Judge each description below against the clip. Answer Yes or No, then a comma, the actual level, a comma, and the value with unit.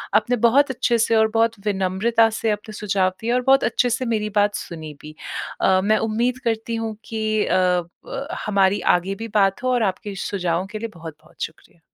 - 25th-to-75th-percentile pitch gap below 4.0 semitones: Yes, average, 3.4 semitones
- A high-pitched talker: Yes, high, 215 Hz